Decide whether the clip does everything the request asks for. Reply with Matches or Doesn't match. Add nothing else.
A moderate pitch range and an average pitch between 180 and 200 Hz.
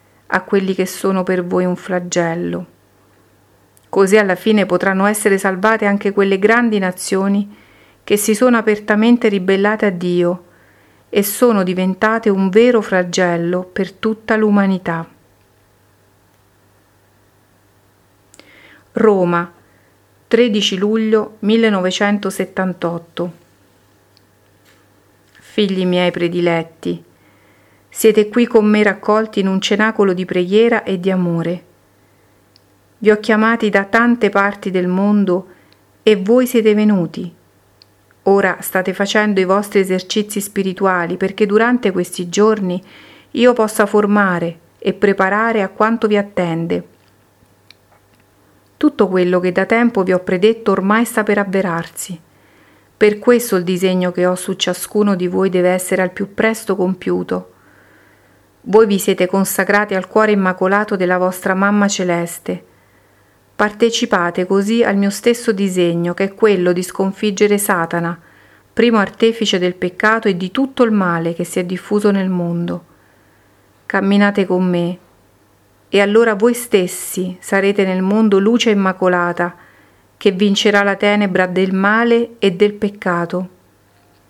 Matches